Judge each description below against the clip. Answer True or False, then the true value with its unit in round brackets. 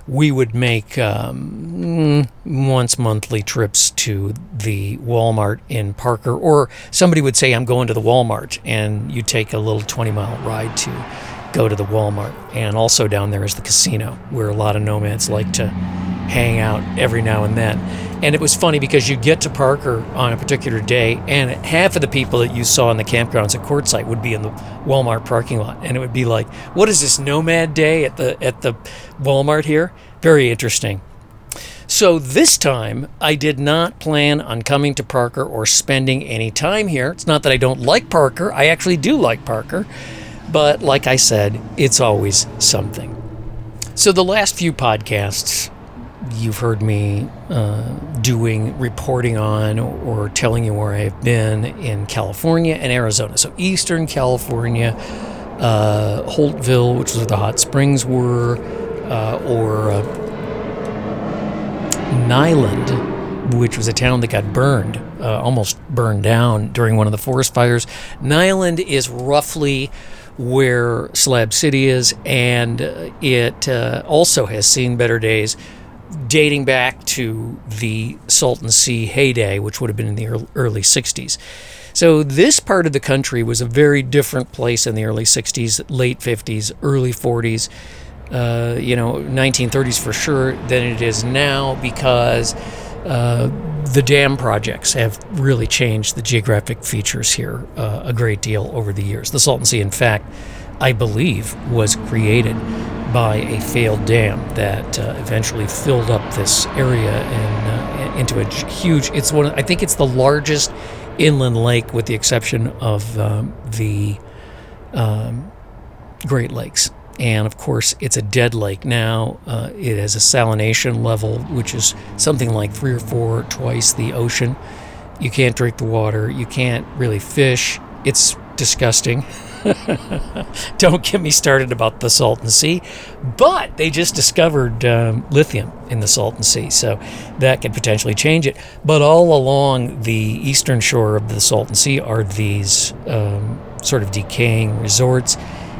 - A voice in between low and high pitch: False (120 Hz)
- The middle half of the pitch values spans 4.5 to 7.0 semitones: False (3.6 semitones)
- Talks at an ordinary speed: True (160 wpm)